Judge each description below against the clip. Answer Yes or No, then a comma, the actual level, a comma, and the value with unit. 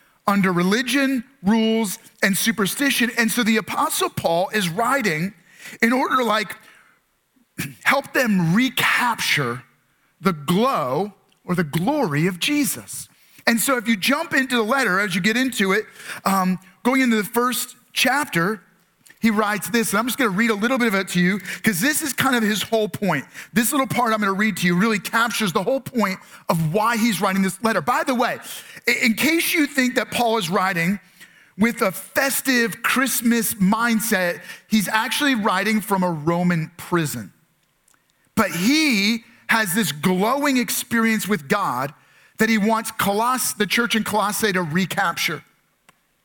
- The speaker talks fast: No, average, 165 wpm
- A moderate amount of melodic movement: Yes, average, 4.0 semitones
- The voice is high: Yes, high, 220 Hz